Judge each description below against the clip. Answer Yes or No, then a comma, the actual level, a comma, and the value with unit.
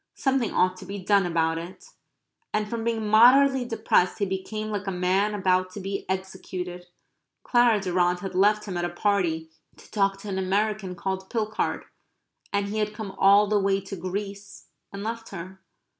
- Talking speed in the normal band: Yes, average, 180 wpm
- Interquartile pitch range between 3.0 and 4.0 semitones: No, narrow, 2.4 semitones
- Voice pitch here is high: Yes, high, 195 Hz